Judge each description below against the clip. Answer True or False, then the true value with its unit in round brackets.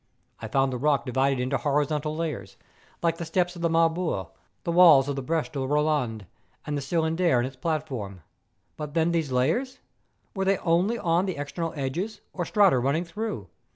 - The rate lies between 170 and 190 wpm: True (185 wpm)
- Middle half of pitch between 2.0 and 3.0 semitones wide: False (4.1 semitones)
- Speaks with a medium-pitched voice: True (155 Hz)